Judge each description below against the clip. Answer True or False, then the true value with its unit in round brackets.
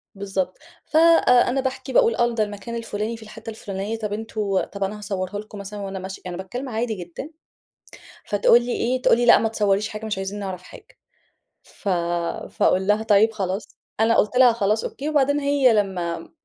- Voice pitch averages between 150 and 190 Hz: False (215 Hz)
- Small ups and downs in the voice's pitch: False (3.3 semitones)